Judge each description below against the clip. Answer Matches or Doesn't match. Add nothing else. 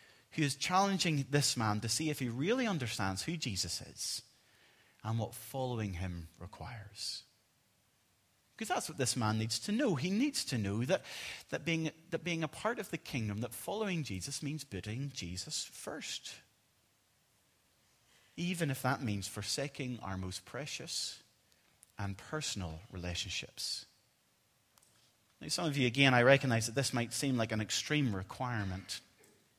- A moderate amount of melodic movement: Doesn't match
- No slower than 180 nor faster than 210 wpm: Doesn't match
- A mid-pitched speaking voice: Doesn't match